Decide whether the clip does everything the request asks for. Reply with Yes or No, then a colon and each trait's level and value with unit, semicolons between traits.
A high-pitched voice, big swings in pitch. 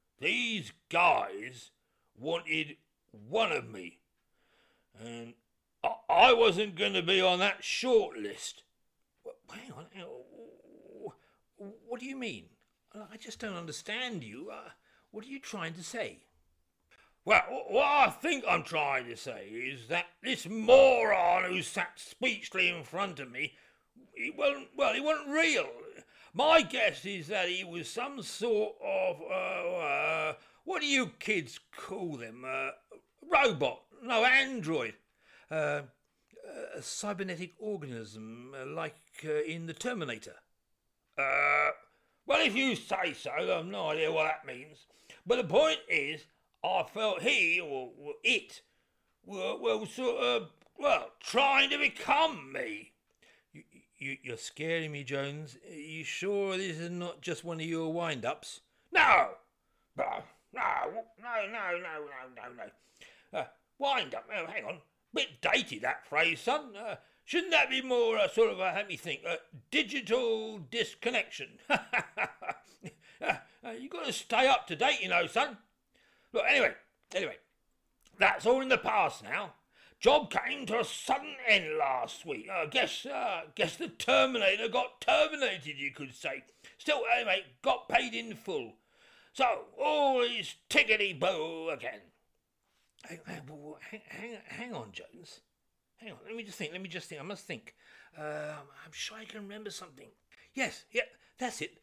Yes: high, 205 Hz; wide, 8.9 semitones